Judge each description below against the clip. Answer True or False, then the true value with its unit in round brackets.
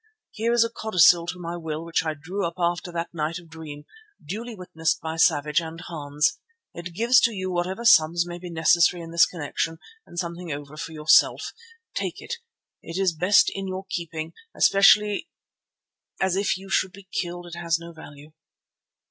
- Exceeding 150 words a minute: True (180 wpm)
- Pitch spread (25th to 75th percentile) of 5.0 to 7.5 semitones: False (2.6 semitones)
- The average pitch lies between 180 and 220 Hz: False (170 Hz)